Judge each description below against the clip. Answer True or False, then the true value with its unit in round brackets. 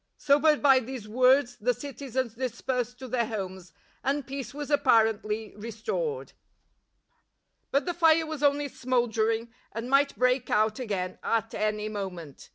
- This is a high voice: True (245 Hz)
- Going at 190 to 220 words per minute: False (160 wpm)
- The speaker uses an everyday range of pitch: True (4.3 semitones)